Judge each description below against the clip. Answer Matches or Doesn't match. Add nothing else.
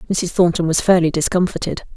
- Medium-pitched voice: Matches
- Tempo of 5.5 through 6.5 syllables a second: Matches